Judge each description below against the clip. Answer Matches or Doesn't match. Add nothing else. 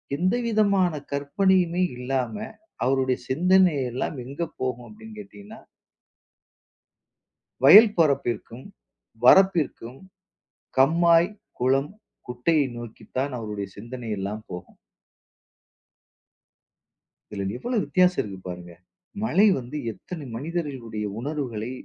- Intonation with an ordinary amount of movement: Doesn't match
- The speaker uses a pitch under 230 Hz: Matches